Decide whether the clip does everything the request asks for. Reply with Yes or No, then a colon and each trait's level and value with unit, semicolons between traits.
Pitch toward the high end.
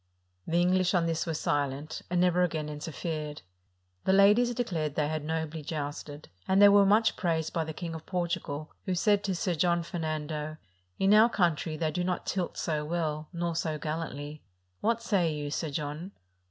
No: medium, 165 Hz